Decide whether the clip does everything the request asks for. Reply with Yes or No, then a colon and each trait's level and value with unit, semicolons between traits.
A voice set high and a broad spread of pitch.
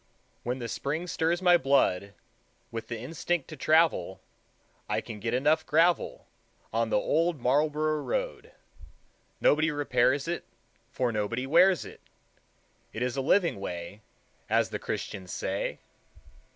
No: medium, 140 Hz; wide, 5.9 semitones